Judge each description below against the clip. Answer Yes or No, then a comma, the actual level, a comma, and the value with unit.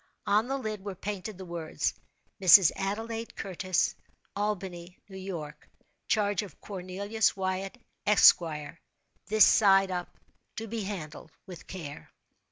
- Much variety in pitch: No, narrow, 2.5 semitones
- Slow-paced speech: Yes, slow, 120 wpm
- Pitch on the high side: Yes, high, 195 Hz